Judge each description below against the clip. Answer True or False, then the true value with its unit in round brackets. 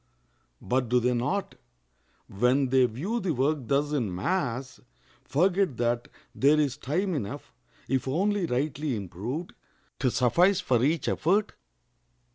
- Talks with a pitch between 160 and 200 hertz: False (135 Hz)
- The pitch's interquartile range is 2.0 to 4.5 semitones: False (5.5 semitones)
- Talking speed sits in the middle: False (130 wpm)